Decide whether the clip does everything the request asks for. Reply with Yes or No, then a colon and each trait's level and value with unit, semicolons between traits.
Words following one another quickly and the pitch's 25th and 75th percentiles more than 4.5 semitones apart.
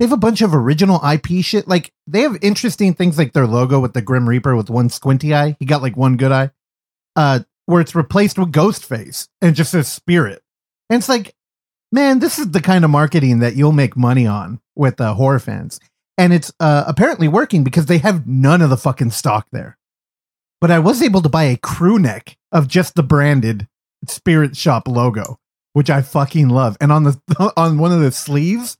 Yes: fast, 215 wpm; average, 5.3 semitones